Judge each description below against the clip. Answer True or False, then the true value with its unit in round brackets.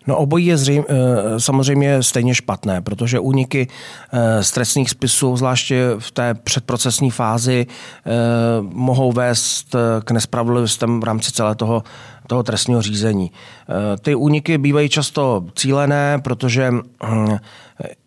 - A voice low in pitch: True (125 Hz)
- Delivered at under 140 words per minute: True (115 wpm)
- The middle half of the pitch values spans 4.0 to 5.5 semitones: False (2.8 semitones)